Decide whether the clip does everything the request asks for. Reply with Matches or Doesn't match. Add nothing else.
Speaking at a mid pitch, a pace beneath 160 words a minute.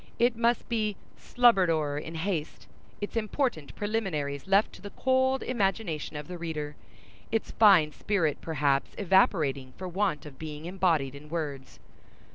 Matches